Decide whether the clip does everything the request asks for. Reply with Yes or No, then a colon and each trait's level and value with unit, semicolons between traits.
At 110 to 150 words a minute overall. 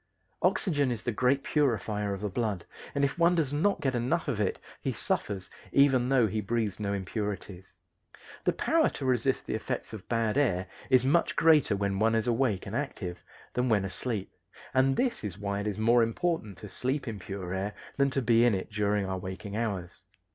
No: average, 200 wpm